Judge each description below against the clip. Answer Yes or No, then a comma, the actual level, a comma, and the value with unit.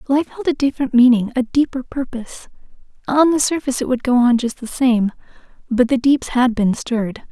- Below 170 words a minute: No, average, 195 wpm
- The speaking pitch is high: Yes, very high, 250 Hz